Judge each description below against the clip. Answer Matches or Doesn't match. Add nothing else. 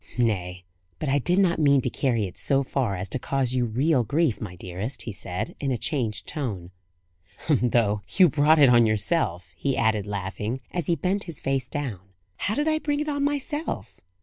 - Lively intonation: Matches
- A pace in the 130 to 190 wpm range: Doesn't match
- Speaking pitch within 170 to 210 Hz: Doesn't match